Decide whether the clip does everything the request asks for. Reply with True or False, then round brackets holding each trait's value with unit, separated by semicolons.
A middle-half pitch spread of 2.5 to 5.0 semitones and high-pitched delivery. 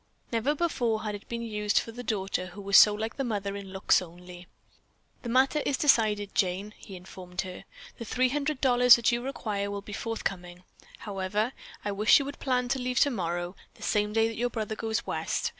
True (3.8 semitones; 215 Hz)